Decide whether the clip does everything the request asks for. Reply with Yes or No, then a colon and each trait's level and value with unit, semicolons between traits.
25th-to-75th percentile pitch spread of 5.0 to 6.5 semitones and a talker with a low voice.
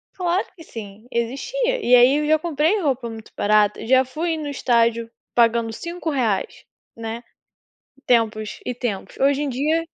No: wide, 5.4 semitones; very high, 250 Hz